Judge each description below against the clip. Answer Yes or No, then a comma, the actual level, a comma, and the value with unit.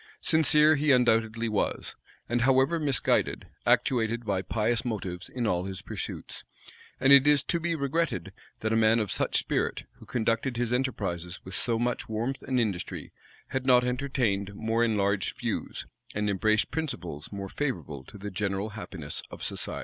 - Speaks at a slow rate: No, average, 165 wpm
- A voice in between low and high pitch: No, low, 115 Hz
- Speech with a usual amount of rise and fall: Yes, average, 4.7 semitones